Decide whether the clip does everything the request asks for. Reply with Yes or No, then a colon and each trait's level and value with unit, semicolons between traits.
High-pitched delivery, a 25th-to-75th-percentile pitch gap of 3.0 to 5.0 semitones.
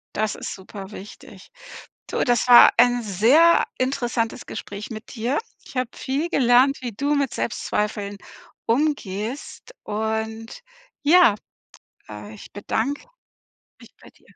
Yes: high, 235 Hz; average, 4.5 semitones